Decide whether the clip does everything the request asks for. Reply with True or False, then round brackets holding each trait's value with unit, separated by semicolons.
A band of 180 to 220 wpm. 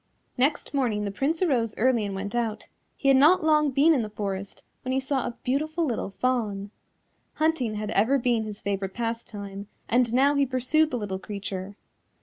True (185 wpm)